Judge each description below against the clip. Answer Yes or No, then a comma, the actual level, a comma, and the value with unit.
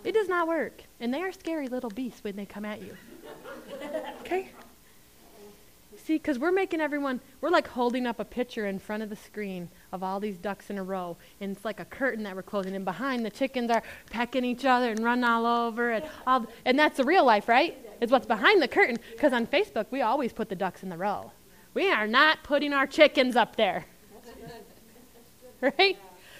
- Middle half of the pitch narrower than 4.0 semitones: No, average, 5.0 semitones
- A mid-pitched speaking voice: No, high, 240 Hz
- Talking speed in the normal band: No, fast, 210 wpm